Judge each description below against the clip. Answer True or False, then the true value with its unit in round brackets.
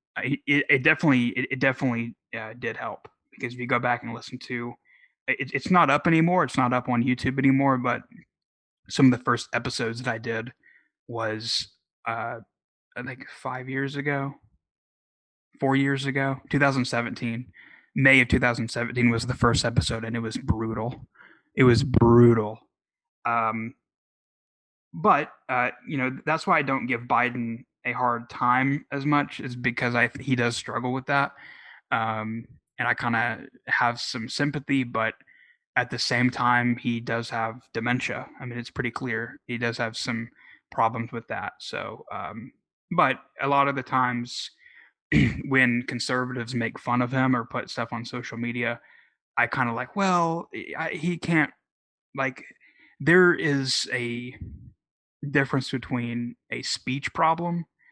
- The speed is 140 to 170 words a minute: True (155 wpm)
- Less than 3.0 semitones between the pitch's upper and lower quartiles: True (2.5 semitones)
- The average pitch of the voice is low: True (125 Hz)